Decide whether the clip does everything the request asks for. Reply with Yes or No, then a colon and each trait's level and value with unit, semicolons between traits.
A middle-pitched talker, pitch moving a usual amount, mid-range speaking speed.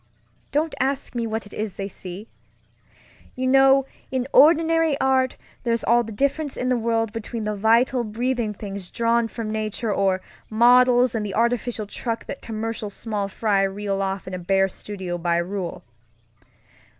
No: high, 225 Hz; average, 3.7 semitones; average, 160 wpm